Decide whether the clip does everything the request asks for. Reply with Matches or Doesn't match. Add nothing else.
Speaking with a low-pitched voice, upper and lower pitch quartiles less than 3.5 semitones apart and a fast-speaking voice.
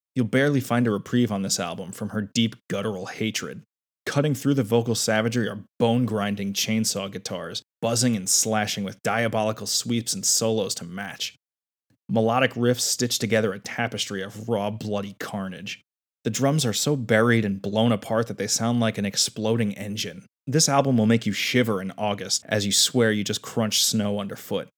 Doesn't match